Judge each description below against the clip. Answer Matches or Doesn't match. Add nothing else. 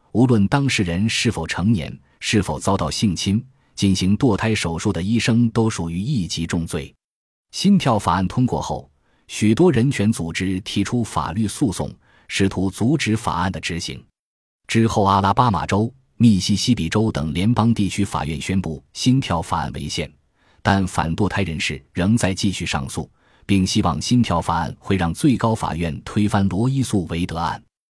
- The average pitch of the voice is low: Matches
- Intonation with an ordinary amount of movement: Matches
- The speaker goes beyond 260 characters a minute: Doesn't match